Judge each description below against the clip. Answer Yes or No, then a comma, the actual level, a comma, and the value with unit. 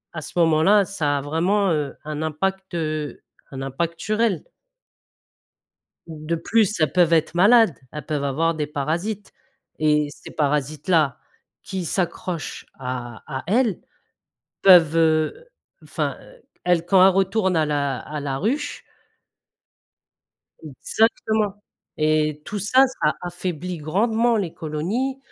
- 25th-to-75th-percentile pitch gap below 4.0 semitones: No, average, 4.5 semitones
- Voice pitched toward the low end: No, medium, 165 Hz